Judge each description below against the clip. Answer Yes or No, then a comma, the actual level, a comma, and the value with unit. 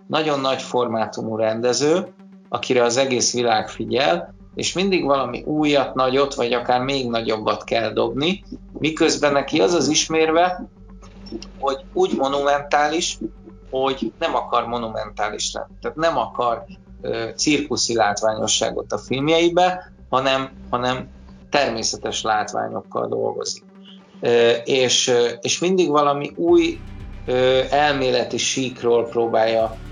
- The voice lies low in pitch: Yes, low, 130 Hz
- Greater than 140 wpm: No, average, 115 wpm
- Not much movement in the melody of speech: No, average, 4.5 semitones